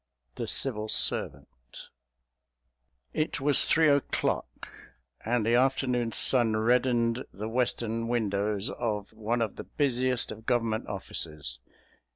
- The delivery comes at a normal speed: No, slow, 115 wpm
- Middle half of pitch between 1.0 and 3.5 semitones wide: Yes, average, 2.8 semitones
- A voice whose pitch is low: Yes, low, 115 Hz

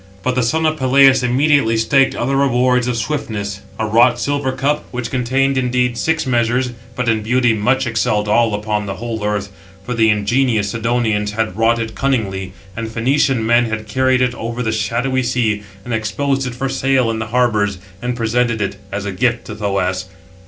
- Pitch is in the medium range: No, low, 120 Hz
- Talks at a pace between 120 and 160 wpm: No, average, 190 wpm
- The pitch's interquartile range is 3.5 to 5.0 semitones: No, average, 2.8 semitones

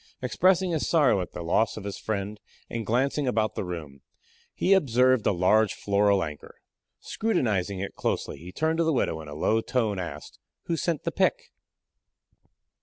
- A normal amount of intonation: No, wide, 6.6 semitones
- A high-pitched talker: No, low, 110 Hz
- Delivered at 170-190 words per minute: Yes, average, 180 wpm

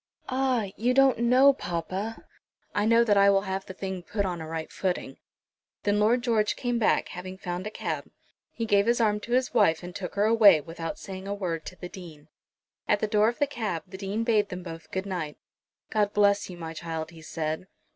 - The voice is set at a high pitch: Yes, high, 200 Hz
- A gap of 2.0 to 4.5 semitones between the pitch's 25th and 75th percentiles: Yes, average, 4.1 semitones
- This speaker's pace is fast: Yes, fast, 215 wpm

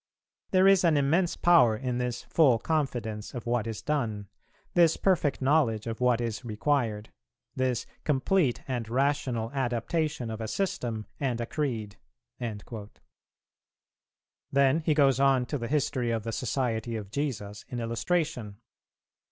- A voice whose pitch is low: Yes, low, 125 Hz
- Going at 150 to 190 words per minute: No, average, 140 wpm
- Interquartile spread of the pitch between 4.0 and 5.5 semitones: Yes, average, 4.4 semitones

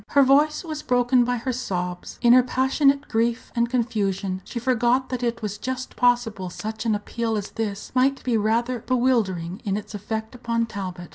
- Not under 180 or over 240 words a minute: Yes, average, 185 wpm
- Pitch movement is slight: No, average, 3.4 semitones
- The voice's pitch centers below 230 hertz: No, high, 235 Hz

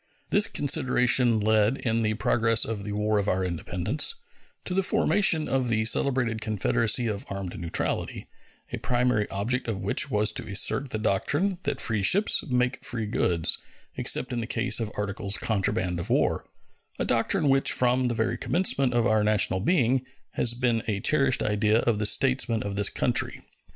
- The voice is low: Yes, low, 115 Hz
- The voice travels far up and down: No, average, 3.4 semitones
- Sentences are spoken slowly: No, average, 175 wpm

